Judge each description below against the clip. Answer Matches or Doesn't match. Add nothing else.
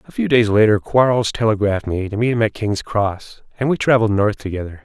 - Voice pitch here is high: Doesn't match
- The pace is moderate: Doesn't match